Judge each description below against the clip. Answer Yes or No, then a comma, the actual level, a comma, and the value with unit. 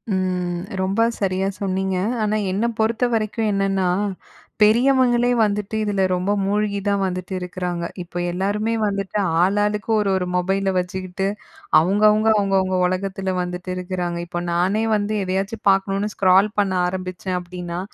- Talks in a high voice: Yes, high, 195 Hz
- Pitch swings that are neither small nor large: No, narrow, 2.2 semitones